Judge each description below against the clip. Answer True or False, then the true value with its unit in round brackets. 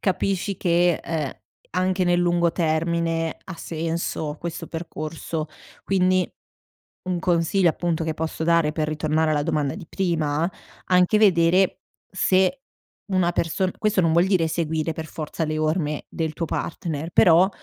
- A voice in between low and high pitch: True (170 Hz)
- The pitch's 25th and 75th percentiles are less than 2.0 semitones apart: False (2.4 semitones)